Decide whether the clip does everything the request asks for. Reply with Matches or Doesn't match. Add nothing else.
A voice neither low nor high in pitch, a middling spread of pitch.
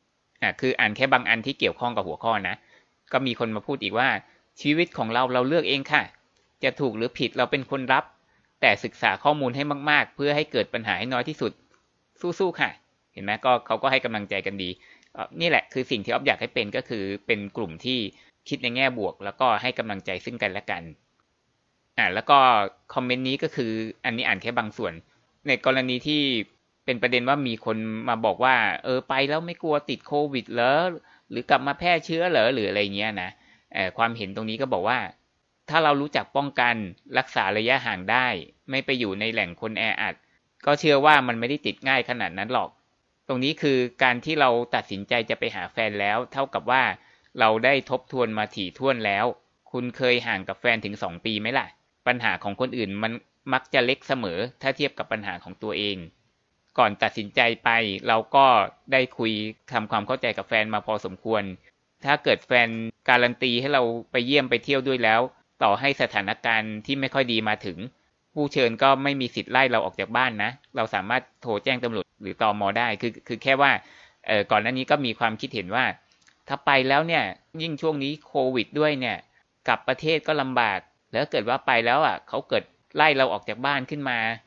Doesn't match